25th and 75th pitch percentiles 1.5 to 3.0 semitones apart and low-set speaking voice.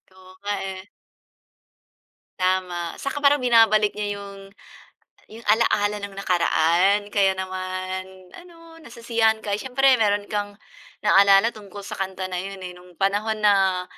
No: average, 2.7 semitones; high, 200 Hz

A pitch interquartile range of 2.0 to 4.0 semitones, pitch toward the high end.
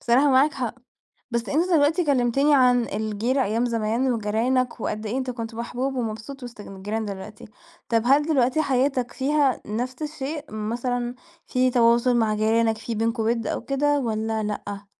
Yes: average, 3.1 semitones; high, 240 Hz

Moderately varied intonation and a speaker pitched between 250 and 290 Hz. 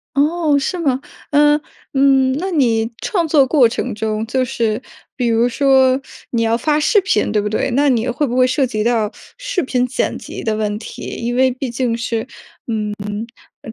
Yes: average, 3.8 semitones; very high, 255 Hz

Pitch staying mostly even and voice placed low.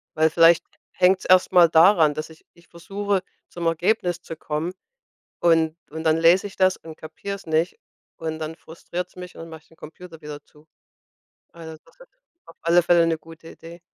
No: narrow, 1.9 semitones; medium, 165 Hz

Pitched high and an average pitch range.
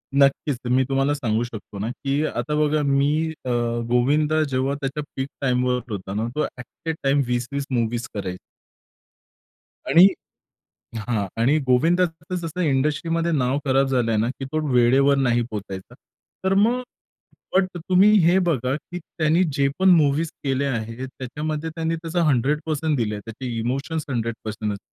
No: low, 135 Hz; average, 4.3 semitones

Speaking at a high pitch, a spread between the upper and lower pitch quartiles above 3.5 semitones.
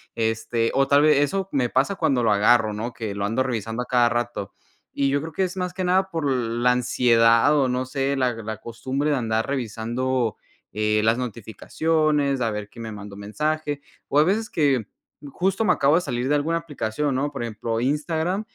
No: low, 130 Hz; average, 4.5 semitones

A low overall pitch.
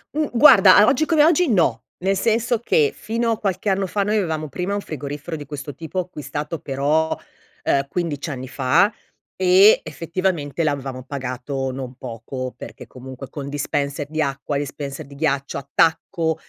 No: medium, 150 Hz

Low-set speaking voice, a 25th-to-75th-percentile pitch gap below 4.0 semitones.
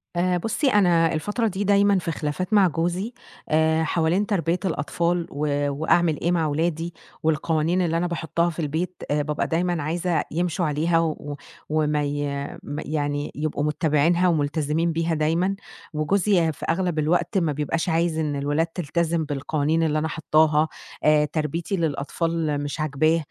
No: medium, 160 Hz; narrow, 2.4 semitones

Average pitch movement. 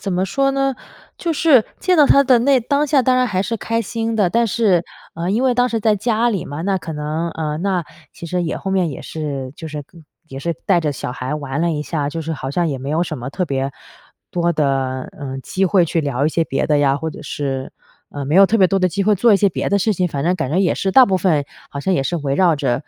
No: wide, 6.3 semitones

